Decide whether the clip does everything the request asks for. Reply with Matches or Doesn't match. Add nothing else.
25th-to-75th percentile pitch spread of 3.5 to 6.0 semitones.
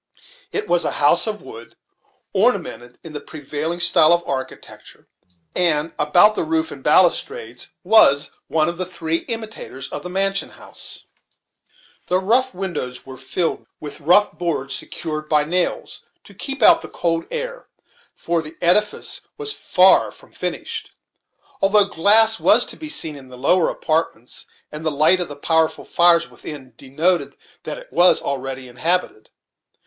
Matches